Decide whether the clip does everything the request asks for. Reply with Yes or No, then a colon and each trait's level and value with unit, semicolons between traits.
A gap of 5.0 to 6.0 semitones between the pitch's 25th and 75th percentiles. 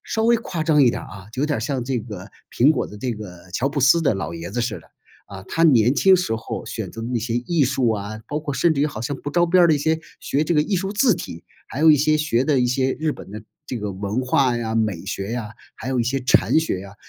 Yes: wide, 5.6 semitones